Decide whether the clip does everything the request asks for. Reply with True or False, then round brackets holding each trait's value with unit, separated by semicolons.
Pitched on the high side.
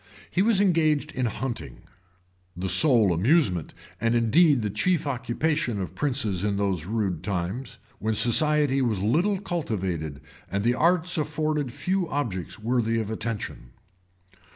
False (120 Hz)